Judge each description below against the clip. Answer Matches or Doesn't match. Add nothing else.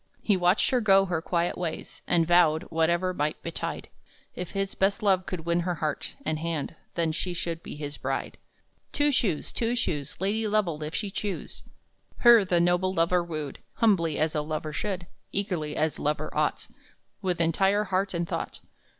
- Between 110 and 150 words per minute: Doesn't match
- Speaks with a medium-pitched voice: Matches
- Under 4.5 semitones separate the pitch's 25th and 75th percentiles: Matches